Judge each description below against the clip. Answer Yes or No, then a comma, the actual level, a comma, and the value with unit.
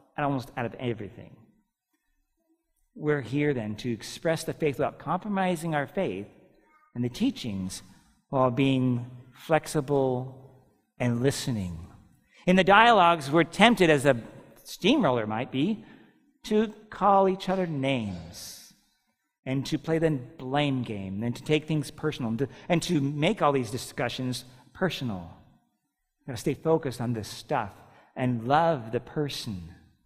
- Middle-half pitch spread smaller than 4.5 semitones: No, average, 5.3 semitones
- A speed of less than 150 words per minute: Yes, average, 140 wpm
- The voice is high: No, medium, 140 Hz